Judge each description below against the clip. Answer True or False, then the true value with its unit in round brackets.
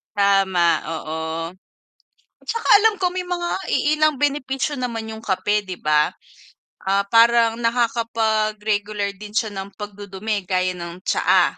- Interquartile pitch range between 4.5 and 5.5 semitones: False (3.6 semitones)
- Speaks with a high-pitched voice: True (215 Hz)